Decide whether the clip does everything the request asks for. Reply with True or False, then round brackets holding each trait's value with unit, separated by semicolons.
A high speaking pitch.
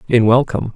False (120 Hz)